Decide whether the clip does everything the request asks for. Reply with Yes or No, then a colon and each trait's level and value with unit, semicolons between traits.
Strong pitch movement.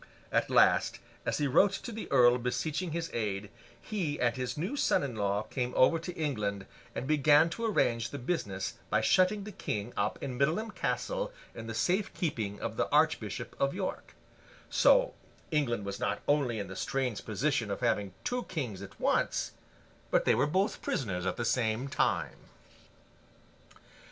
Yes: wide, 7.4 semitones